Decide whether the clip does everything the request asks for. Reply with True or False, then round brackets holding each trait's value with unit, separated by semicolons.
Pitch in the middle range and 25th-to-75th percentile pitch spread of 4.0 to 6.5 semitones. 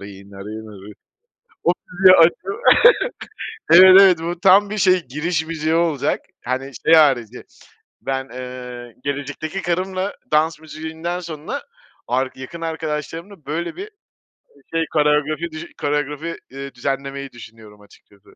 True (150 Hz; 4.4 semitones)